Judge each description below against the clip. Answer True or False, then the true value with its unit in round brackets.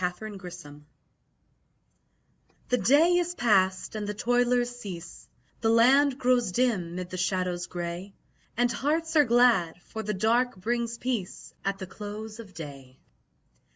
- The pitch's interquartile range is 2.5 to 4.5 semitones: False (5.0 semitones)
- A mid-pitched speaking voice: False (215 Hz)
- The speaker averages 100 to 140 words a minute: True (135 wpm)